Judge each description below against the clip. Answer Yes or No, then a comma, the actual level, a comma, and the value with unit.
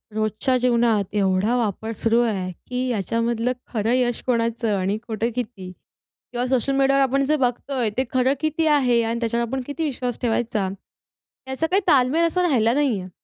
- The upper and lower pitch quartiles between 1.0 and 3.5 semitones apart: Yes, average, 3.0 semitones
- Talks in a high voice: Yes, high, 240 Hz